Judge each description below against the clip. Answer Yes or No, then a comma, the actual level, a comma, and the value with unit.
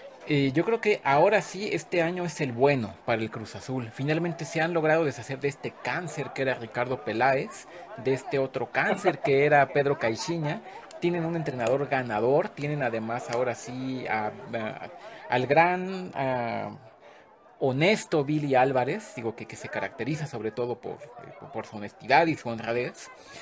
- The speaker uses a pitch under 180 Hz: Yes, low, 135 Hz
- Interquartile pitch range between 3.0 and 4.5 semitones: No, average, 5.3 semitones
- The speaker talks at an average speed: Yes, average, 170 wpm